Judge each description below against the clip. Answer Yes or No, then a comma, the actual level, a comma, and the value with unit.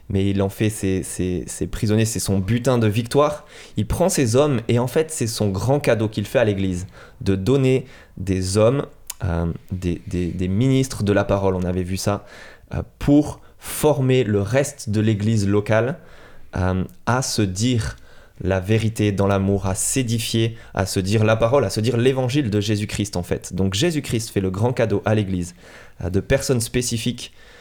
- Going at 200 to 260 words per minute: No, average, 190 wpm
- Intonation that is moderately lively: Yes, average, 4.5 semitones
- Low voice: Yes, low, 110 Hz